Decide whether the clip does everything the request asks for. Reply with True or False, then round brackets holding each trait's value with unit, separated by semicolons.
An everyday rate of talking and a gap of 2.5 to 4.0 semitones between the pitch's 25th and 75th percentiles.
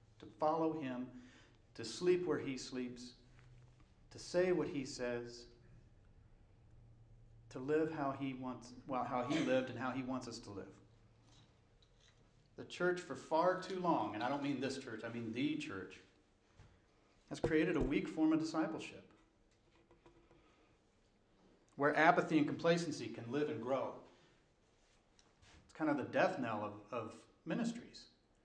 False (145 wpm; 5.2 semitones)